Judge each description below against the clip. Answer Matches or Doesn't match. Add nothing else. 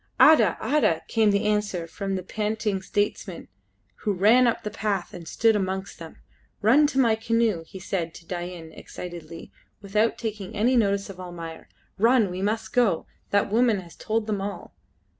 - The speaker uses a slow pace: Doesn't match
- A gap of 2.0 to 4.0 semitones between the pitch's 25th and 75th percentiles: Matches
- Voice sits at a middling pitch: Doesn't match